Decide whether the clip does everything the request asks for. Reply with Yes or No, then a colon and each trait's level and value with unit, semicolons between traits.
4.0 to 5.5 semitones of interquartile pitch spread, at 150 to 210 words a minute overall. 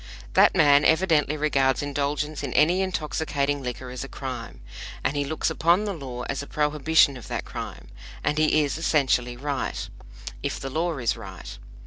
No: narrow, 2.6 semitones; average, 170 wpm